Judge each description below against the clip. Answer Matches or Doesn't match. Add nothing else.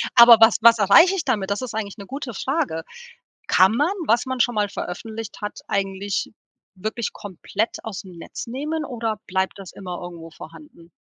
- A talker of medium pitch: Doesn't match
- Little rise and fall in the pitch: Doesn't match